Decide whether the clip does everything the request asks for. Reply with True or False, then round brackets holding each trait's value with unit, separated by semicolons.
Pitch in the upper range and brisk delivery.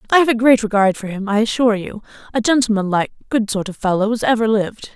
True (220 Hz; 240 wpm)